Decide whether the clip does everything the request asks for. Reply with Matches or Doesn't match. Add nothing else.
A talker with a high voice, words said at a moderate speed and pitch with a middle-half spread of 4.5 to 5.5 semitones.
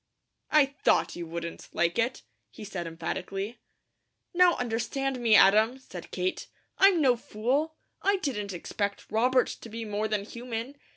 Matches